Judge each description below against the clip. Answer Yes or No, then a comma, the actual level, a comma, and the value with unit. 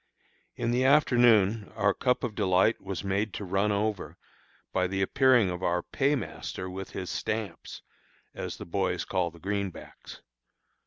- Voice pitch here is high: No, low, 100 Hz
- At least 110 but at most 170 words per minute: Yes, average, 150 wpm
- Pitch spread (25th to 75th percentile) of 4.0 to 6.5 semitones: No, average, 3.5 semitones